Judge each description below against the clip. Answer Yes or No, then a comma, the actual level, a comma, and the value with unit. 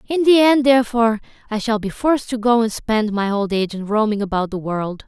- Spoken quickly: Yes, fast, 235 wpm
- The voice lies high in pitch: Yes, high, 225 Hz